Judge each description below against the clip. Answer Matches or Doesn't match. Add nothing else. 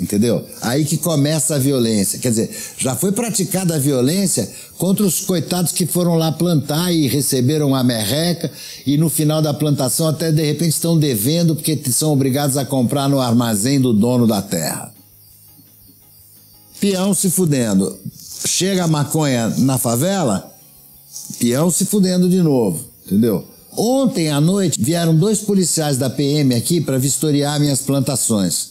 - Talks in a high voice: Doesn't match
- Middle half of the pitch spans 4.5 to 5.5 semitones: Matches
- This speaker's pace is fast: Doesn't match